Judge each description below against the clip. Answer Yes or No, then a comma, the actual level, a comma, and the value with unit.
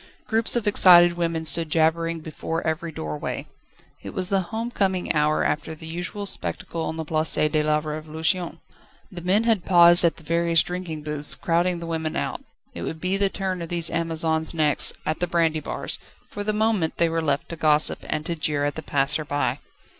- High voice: No, medium, 165 Hz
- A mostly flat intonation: Yes, narrow, 2.3 semitones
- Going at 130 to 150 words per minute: No, average, 200 wpm